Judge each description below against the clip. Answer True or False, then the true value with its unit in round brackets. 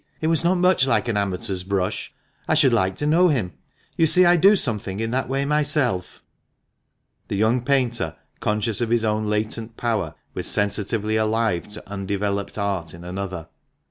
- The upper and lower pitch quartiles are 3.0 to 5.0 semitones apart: False (5.4 semitones)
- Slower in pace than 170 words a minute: False (175 wpm)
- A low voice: True (110 Hz)